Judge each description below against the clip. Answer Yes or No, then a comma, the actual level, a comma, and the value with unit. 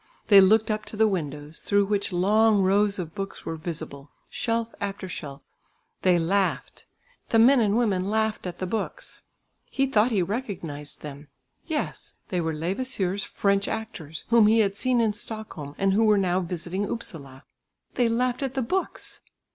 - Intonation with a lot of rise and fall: No, average, 4.2 semitones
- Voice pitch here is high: Yes, high, 200 Hz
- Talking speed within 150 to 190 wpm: Yes, average, 170 wpm